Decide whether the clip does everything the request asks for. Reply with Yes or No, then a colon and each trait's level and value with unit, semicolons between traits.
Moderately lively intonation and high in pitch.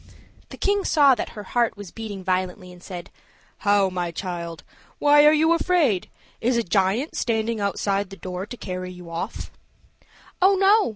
No: wide, 6.8 semitones; high, 205 Hz